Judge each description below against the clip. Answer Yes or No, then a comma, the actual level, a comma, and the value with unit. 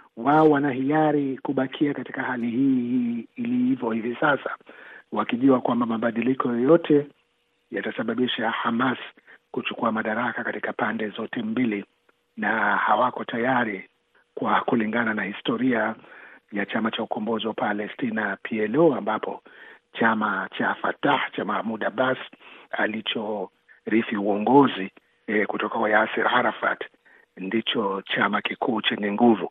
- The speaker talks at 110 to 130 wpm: Yes, average, 115 wpm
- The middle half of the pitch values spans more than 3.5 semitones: Yes, average, 4.1 semitones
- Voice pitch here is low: Yes, low, 130 Hz